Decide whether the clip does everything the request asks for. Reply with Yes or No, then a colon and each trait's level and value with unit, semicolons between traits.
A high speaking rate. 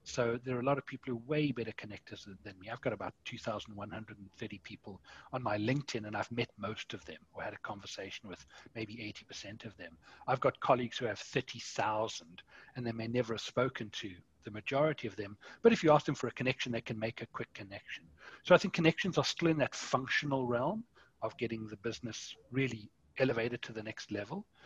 Yes: fast, 215 wpm